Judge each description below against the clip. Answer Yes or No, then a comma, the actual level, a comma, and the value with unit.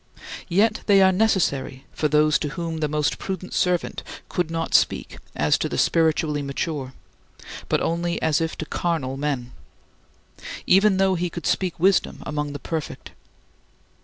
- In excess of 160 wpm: No, average, 155 wpm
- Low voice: No, medium, 165 Hz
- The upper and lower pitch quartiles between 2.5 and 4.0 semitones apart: Yes, average, 3.4 semitones